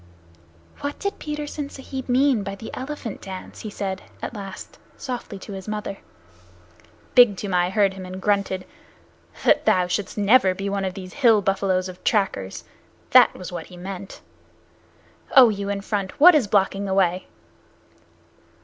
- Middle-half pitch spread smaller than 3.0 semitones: No, average, 3.6 semitones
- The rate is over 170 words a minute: No, average, 160 wpm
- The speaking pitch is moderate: No, high, 200 Hz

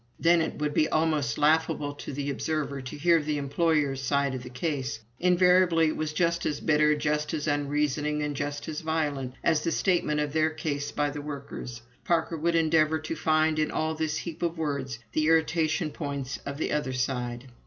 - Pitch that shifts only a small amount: Yes, narrow, 1.9 semitones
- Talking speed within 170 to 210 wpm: Yes, average, 195 wpm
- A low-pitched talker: No, medium, 150 Hz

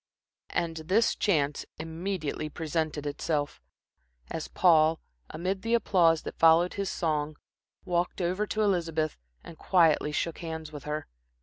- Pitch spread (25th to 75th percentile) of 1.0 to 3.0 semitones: Yes, average, 2.7 semitones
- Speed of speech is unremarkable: No, slow, 130 wpm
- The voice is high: No, medium, 165 Hz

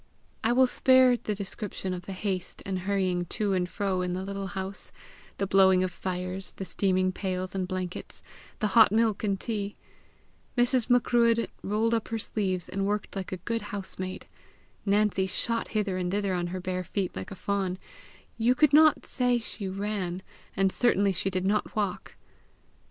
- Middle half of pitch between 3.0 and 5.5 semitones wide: No, narrow, 2.5 semitones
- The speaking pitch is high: Yes, high, 195 Hz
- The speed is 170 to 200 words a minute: Yes, average, 175 wpm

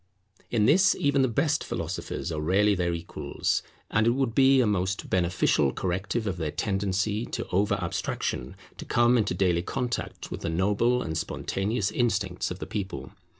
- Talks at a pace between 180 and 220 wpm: No, average, 170 wpm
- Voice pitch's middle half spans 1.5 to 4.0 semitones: No, average, 4.7 semitones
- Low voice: Yes, low, 100 Hz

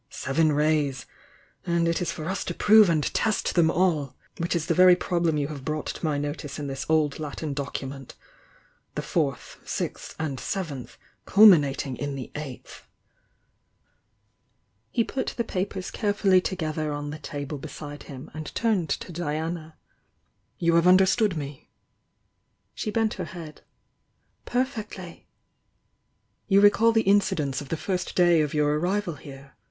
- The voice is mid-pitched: Yes, medium, 160 Hz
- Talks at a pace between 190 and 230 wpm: No, average, 155 wpm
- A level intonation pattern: No, average, 4.2 semitones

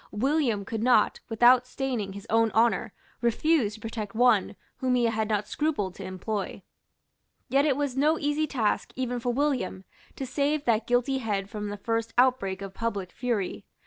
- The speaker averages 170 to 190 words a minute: Yes, average, 175 wpm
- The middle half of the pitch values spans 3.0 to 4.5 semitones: Yes, average, 4.0 semitones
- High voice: Yes, high, 235 Hz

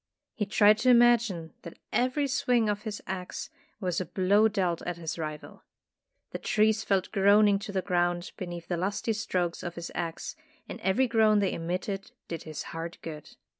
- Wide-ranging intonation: No, average, 3.7 semitones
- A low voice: No, high, 195 Hz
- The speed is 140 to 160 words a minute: No, average, 175 wpm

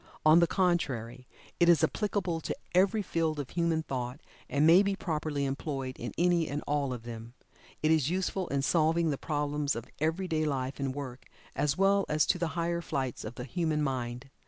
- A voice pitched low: No, medium, 155 Hz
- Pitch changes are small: No, average, 4.1 semitones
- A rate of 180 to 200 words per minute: Yes, average, 195 wpm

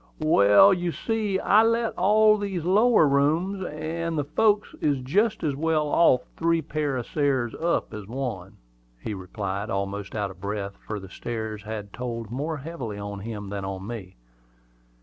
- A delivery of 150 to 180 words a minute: Yes, average, 170 wpm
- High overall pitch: No, medium, 140 Hz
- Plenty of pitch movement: Yes, wide, 8.7 semitones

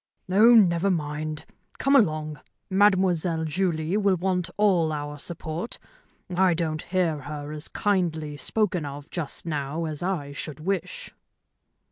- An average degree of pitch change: Yes, average, 3.7 semitones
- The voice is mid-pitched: Yes, medium, 165 Hz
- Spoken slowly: Yes, slow, 130 wpm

